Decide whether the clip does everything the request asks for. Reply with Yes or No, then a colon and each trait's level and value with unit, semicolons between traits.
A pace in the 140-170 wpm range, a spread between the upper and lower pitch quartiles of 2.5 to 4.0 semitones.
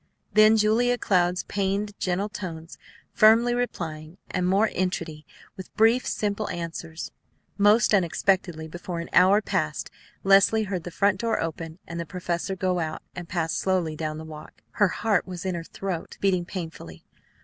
Yes: average, 160 wpm; average, 3.6 semitones